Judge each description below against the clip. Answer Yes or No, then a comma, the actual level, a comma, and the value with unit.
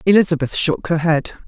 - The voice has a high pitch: No, medium, 165 Hz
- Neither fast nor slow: Yes, average, 165 wpm